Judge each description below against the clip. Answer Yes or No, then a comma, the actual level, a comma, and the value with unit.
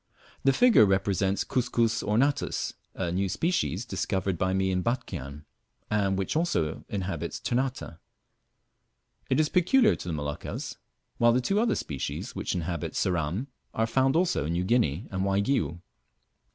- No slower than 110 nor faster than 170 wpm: Yes, average, 145 wpm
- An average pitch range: No, wide, 6.3 semitones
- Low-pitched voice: Yes, low, 100 Hz